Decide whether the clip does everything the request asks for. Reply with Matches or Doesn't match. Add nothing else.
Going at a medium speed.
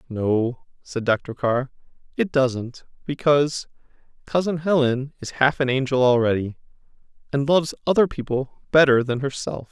Doesn't match